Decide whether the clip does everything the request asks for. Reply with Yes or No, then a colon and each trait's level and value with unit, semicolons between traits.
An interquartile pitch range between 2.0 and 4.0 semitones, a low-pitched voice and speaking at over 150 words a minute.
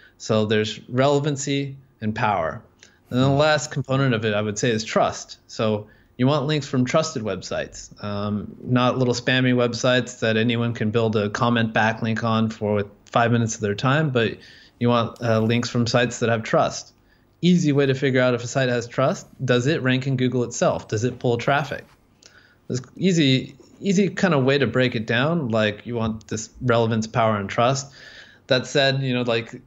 Yes: average, 3.0 semitones; low, 120 Hz; average, 190 wpm